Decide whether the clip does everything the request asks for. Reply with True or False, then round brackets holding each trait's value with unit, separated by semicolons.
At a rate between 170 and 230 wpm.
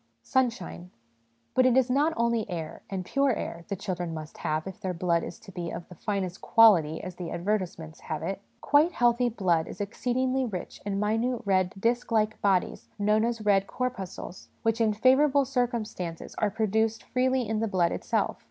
True (190 wpm)